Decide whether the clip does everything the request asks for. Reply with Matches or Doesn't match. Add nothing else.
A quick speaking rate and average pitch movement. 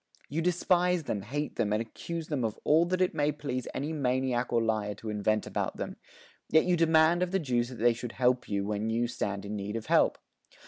Doesn't match